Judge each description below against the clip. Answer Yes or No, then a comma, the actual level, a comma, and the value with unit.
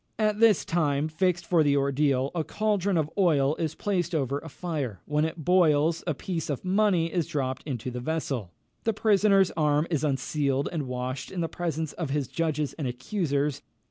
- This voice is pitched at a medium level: Yes, medium, 155 Hz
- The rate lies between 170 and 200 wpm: Yes, average, 185 wpm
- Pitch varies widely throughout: No, average, 4.0 semitones